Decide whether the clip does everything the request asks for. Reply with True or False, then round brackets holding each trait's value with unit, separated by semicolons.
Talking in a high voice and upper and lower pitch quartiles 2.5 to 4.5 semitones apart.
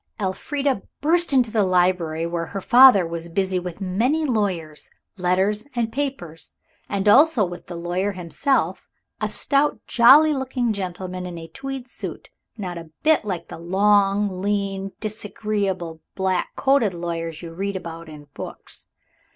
False (195 Hz; 5.2 semitones)